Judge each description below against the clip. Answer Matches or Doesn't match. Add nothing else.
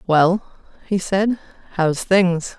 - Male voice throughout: Doesn't match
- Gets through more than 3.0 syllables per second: Doesn't match